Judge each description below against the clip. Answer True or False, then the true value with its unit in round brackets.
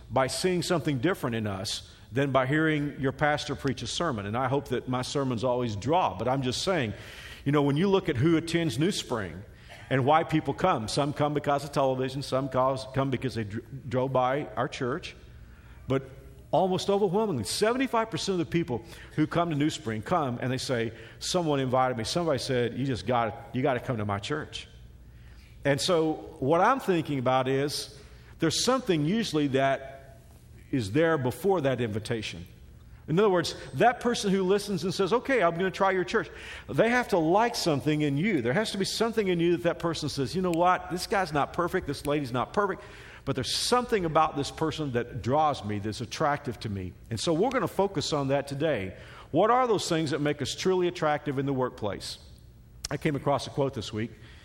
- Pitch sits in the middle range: True (145 Hz)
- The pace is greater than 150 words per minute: True (205 wpm)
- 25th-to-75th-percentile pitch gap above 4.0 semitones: True (5.3 semitones)